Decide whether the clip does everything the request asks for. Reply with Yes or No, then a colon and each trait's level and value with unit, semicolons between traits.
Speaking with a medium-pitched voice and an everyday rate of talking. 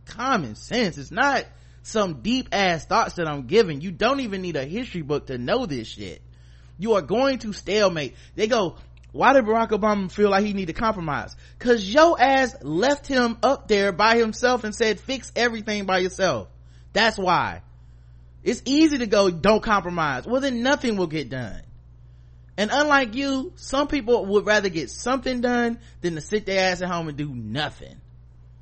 No: high, 195 Hz; average, 185 wpm